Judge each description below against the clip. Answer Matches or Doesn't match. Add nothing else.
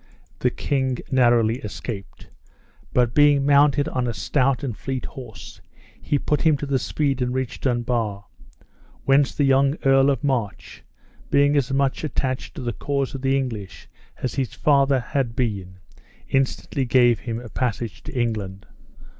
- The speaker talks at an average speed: Matches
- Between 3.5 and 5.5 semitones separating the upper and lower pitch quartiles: Doesn't match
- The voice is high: Doesn't match